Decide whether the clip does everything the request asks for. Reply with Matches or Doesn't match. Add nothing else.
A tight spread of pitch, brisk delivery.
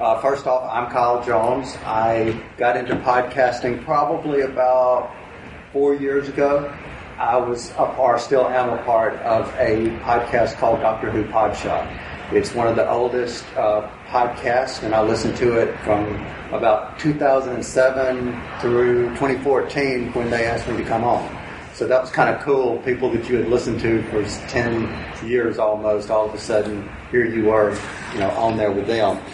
Doesn't match